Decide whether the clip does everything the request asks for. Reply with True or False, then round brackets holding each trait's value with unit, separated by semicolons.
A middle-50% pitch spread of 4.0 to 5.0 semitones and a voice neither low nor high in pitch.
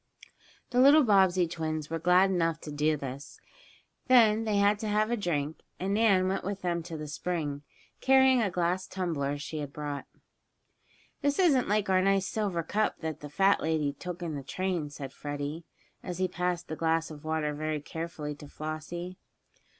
True (4.3 semitones; 170 Hz)